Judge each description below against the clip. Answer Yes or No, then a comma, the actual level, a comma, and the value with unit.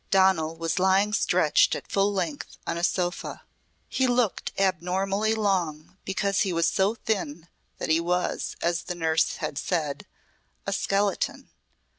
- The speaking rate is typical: Yes, average, 145 wpm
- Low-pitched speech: No, high, 190 Hz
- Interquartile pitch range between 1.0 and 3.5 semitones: Yes, average, 3.0 semitones